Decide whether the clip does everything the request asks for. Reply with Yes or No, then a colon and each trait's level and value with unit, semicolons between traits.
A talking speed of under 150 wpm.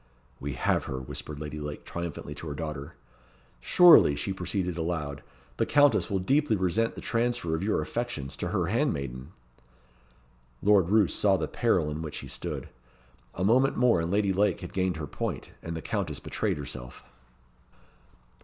No: average, 165 wpm